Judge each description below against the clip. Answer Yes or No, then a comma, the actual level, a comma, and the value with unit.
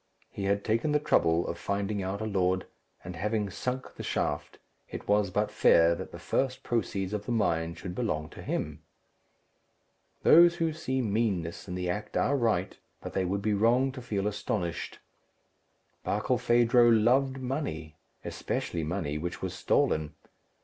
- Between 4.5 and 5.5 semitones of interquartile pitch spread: Yes, average, 5.1 semitones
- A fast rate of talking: No, average, 160 wpm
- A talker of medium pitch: No, low, 100 Hz